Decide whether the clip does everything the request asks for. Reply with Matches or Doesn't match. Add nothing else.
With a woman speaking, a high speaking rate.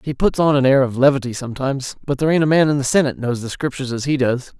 Doesn't match